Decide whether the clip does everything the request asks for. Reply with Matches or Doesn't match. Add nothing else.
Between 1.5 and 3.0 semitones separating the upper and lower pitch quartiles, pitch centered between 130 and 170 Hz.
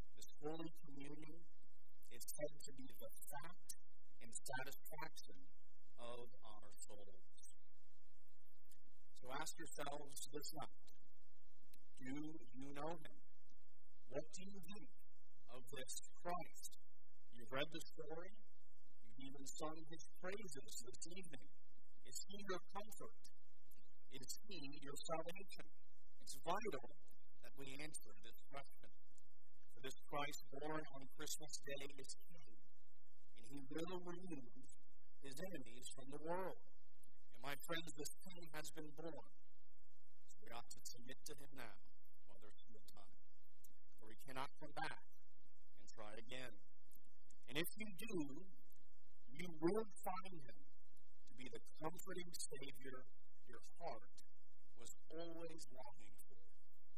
Doesn't match